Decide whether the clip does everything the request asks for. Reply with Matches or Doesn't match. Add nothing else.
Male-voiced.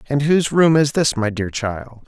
Matches